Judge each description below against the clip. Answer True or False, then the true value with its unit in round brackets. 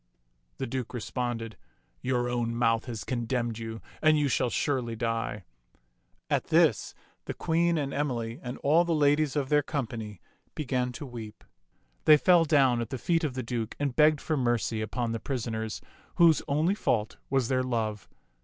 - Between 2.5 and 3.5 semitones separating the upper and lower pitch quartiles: False (4.1 semitones)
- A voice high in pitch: False (125 Hz)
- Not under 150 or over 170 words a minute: False (180 wpm)